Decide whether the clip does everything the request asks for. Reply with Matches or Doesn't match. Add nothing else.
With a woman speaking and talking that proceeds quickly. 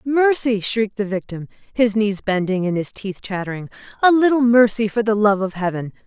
Doesn't match